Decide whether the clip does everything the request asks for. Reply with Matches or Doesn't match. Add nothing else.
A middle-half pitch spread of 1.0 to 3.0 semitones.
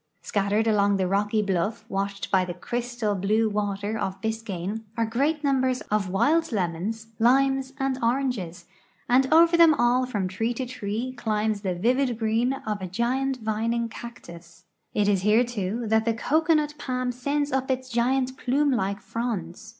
Doesn't match